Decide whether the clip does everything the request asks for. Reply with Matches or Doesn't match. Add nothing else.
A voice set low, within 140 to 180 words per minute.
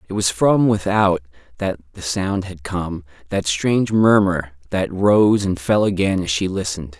Matches